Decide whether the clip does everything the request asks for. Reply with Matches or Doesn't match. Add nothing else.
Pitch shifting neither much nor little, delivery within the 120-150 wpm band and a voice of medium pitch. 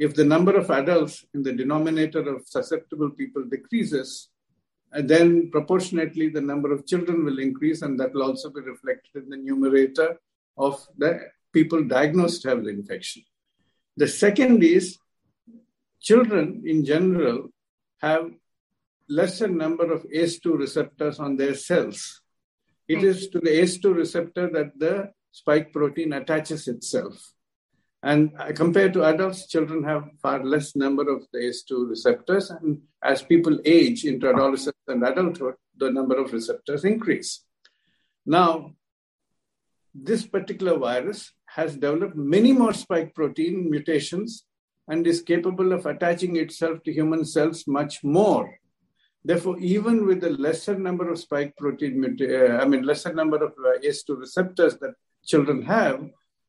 Matches